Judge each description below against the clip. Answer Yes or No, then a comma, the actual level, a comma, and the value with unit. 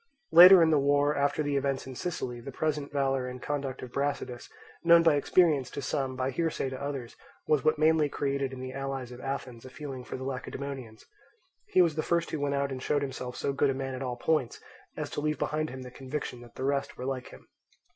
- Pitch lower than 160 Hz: Yes, medium, 140 Hz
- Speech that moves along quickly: Yes, fast, 235 wpm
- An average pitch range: No, narrow, 2.3 semitones